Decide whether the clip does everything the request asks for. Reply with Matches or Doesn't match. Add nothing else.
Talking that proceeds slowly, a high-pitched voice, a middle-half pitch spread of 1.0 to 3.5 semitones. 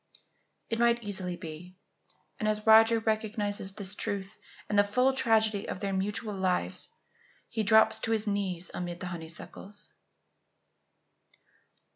Matches